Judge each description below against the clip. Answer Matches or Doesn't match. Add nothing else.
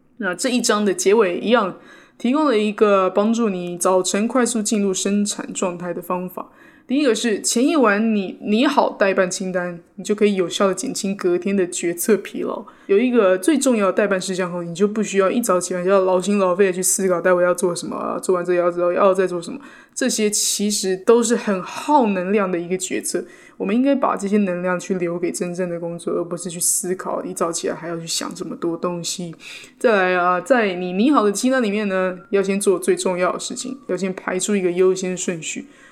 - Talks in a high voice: Matches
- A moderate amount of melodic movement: Matches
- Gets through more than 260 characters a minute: Matches